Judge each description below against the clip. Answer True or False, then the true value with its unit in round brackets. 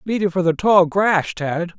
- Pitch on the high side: False (180 Hz)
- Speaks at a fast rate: True (235 wpm)